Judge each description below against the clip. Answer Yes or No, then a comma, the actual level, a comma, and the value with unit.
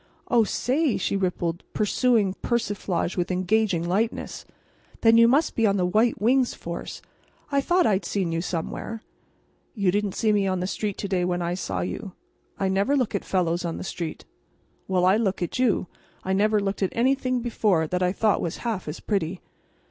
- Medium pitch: No, high, 195 Hz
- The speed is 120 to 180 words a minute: No, average, 195 wpm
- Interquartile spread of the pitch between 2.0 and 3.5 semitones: No, average, 4.0 semitones